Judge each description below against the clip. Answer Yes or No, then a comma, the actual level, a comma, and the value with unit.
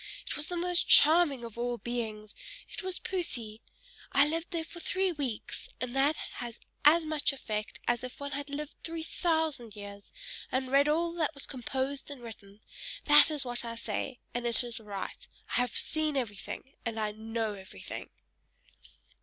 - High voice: Yes, very high, 265 Hz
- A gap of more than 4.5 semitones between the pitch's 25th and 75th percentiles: Yes, average, 5.2 semitones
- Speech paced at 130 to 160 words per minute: No, average, 175 wpm